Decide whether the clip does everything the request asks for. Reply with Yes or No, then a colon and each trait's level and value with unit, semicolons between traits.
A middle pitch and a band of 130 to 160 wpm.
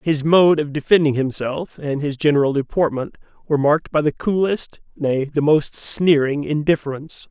Yes: medium, 150 Hz; average, 155 wpm